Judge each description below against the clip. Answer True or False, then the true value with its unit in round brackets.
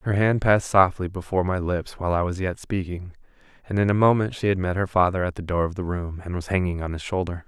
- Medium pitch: False (90 Hz)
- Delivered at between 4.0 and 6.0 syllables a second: False (6.3 syllables/s)